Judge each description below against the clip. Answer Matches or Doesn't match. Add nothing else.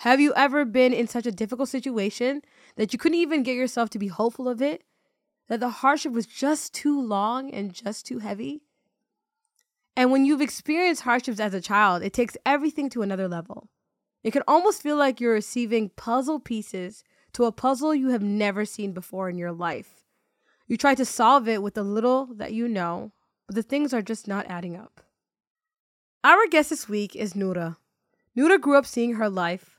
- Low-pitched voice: Doesn't match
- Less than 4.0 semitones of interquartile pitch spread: Doesn't match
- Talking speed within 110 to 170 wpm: Doesn't match